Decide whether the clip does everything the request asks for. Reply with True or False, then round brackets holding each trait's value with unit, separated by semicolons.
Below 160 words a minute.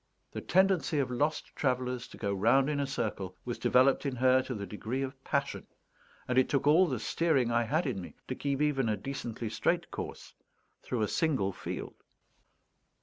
False (190 wpm)